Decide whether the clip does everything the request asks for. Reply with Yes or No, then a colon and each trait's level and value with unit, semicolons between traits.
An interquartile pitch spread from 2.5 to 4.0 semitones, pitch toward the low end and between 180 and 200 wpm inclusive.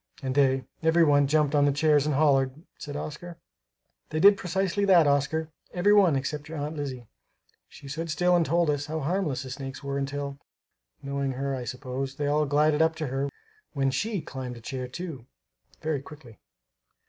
No: average, 2.8 semitones; medium, 145 Hz; average, 185 wpm